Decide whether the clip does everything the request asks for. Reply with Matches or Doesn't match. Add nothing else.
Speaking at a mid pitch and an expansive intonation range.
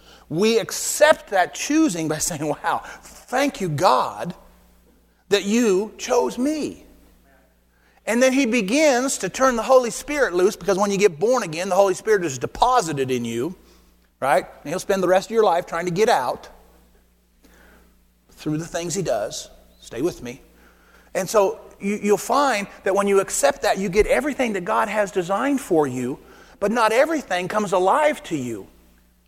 Doesn't match